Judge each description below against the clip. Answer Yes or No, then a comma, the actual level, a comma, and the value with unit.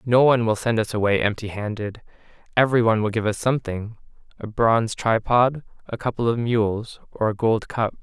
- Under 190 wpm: Yes, average, 180 wpm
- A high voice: No, low, 115 Hz